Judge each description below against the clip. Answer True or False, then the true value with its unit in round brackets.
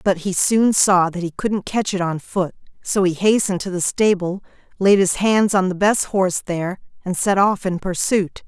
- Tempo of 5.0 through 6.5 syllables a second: False (4.8 syllables/s)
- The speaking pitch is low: False (190 Hz)